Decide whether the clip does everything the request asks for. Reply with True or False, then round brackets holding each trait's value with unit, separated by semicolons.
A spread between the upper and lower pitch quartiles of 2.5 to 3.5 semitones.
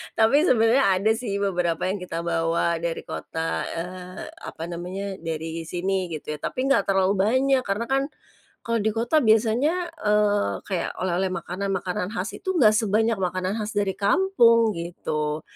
False (4.4 semitones)